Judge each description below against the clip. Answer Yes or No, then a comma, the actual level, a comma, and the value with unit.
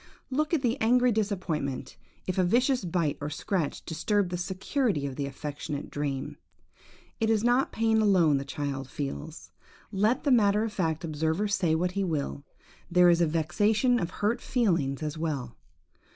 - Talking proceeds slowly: No, average, 165 wpm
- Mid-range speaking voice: Yes, medium, 180 Hz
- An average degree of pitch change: No, wide, 6.5 semitones